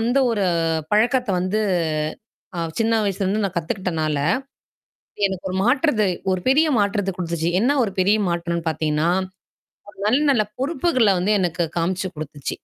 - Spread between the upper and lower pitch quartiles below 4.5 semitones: No, average, 4.8 semitones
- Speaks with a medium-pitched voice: No, high, 195 Hz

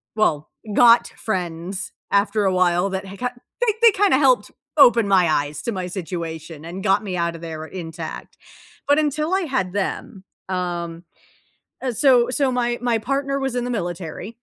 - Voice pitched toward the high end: Yes, high, 195 Hz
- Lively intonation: Yes, wide, 6.2 semitones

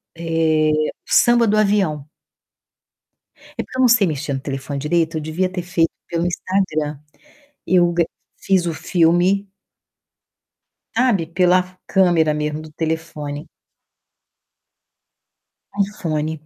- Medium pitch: Yes, medium, 170 Hz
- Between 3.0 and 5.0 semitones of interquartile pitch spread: Yes, average, 3.3 semitones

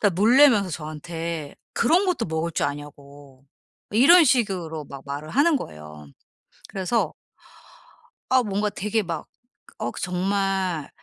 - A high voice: No, medium, 180 Hz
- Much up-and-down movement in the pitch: Yes, wide, 6.8 semitones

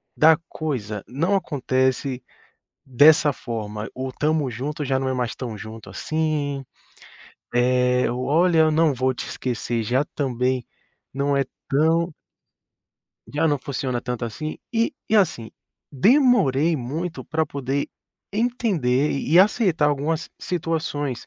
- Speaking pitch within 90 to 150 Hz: Yes, medium, 140 Hz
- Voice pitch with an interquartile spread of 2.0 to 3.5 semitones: No, average, 4.1 semitones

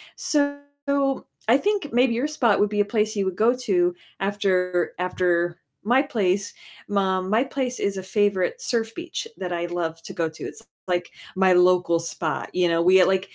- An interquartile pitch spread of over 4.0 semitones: Yes, average, 4.8 semitones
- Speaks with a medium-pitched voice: No, high, 195 Hz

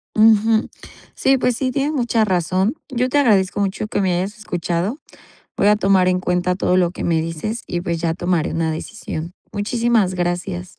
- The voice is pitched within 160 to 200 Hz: Yes, high, 190 Hz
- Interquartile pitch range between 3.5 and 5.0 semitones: Yes, average, 4.1 semitones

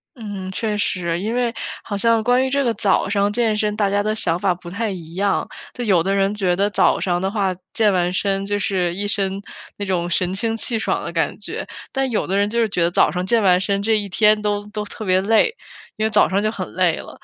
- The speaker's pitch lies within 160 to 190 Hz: No, high, 205 Hz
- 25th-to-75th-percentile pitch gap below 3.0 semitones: Yes, narrow, 2.5 semitones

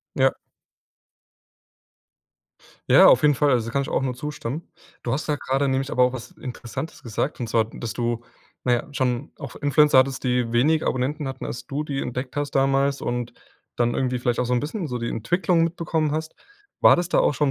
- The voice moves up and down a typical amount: Yes, average, 3.2 semitones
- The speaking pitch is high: No, low, 135 Hz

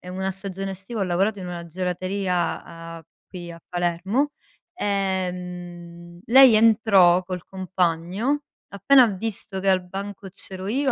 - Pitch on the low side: No, high, 190 Hz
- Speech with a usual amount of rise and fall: No, narrow, 2.3 semitones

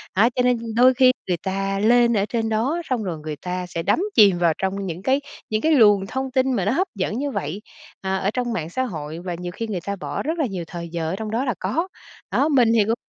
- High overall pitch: Yes, high, 210 Hz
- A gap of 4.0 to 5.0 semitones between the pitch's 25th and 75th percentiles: No, wide, 5.5 semitones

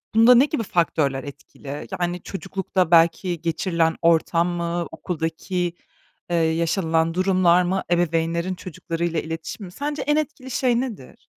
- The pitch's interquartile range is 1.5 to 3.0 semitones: Yes, average, 2.7 semitones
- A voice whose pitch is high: No, medium, 175 Hz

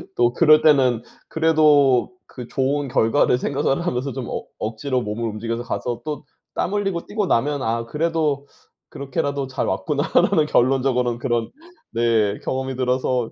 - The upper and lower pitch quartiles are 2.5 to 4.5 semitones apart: Yes, average, 3.7 semitones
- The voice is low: Yes, low, 130 Hz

